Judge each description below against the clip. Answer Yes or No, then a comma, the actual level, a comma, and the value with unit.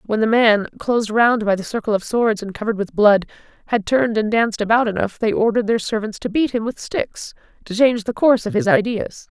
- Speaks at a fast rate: Yes, fast, 230 wpm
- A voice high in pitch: Yes, high, 220 Hz